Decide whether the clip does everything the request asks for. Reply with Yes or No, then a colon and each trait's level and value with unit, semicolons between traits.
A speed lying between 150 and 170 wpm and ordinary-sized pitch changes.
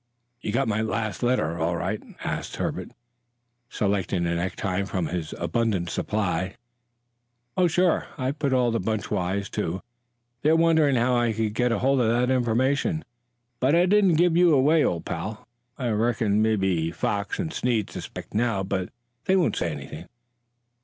No: average, 160 wpm; wide, 6.3 semitones